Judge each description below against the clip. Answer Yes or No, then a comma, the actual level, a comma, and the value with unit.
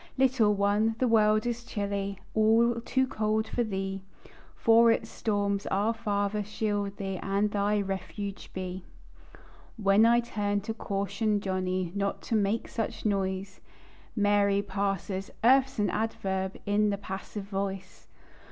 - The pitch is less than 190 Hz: No, high, 205 Hz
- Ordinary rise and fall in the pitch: No, narrow, 2.0 semitones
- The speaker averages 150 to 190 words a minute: No, slow, 135 wpm